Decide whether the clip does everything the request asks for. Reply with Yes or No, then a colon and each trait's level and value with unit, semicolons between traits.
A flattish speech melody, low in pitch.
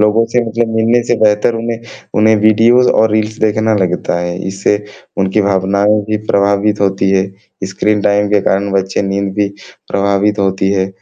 Yes: narrow, 1.9 semitones; low, 105 Hz